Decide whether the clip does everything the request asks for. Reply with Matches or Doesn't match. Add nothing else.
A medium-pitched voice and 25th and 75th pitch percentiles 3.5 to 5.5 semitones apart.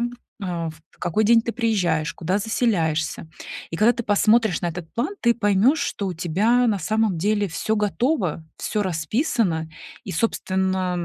Doesn't match